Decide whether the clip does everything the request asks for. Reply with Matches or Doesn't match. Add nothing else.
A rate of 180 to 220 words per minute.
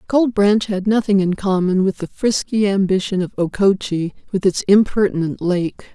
Doesn't match